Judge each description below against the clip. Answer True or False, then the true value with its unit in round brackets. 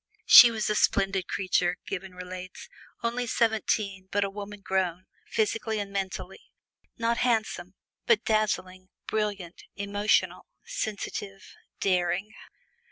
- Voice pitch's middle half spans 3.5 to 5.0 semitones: False (2.6 semitones)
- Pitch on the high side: True (200 Hz)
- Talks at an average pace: False (110 wpm)